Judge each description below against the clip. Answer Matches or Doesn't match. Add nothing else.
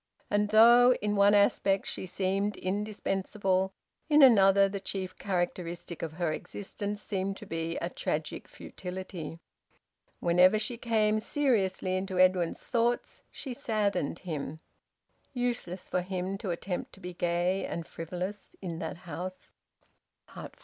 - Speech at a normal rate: Doesn't match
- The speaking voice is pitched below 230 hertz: Matches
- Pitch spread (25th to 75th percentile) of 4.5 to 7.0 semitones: Doesn't match